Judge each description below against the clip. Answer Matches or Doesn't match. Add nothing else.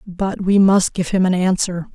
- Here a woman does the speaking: Matches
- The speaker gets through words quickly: Matches